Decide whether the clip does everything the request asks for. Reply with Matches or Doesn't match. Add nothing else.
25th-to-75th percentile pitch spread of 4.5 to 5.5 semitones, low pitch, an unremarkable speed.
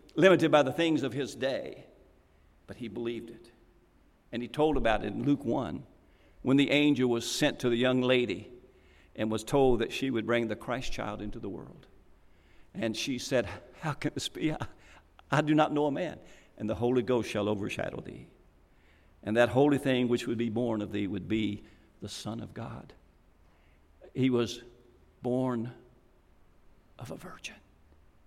Matches